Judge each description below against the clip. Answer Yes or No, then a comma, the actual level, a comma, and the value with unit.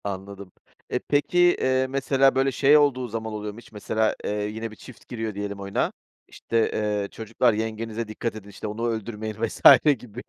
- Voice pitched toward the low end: Yes, low, 110 Hz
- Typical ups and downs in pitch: Yes, average, 3.1 semitones